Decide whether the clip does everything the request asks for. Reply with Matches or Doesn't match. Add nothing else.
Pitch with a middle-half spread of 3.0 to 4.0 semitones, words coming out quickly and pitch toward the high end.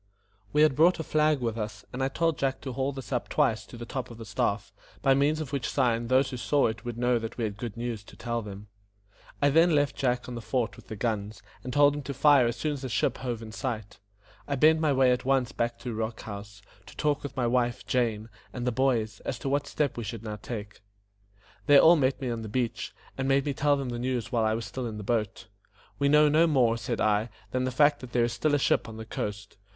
Doesn't match